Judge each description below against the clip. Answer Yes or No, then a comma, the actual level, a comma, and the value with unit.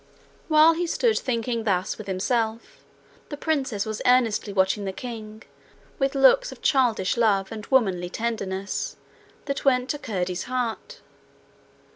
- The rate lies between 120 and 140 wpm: Yes, slow, 135 wpm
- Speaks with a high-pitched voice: Yes, high, 230 Hz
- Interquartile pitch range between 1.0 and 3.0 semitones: No, average, 4.9 semitones